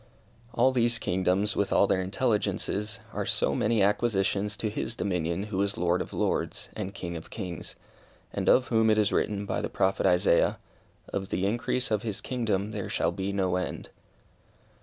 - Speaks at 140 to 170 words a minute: No, average, 180 wpm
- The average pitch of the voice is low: Yes, low, 100 Hz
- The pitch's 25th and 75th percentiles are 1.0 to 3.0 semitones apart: Yes, narrow, 2.4 semitones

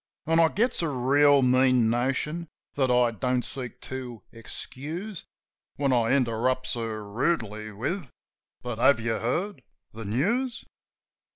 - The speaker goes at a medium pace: No, slow, 130 wpm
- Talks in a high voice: No, low, 130 Hz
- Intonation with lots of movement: No, average, 4.4 semitones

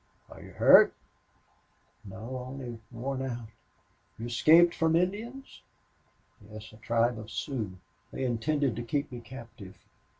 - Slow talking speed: Yes, slow, 130 wpm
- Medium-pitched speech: No, low, 120 Hz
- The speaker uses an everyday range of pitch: Yes, average, 3.8 semitones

